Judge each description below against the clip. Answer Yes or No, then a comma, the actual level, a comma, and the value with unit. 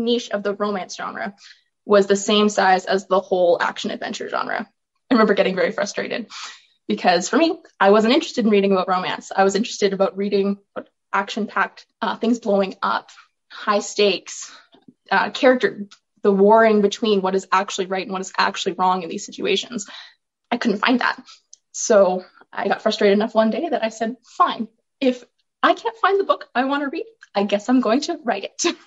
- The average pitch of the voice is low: No, high, 210 Hz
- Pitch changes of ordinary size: Yes, average, 3.8 semitones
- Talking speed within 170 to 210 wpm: Yes, average, 190 wpm